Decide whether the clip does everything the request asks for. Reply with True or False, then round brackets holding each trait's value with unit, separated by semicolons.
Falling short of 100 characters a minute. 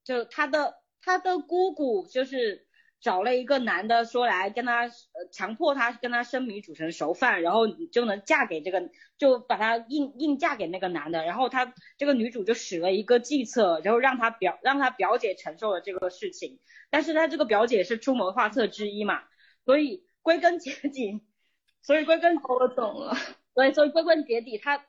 False (280 characters per minute)